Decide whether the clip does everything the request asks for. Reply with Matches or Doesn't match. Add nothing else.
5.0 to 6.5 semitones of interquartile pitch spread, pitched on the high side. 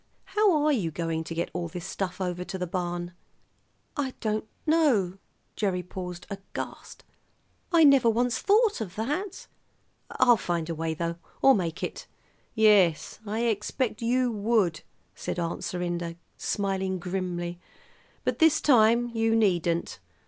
Matches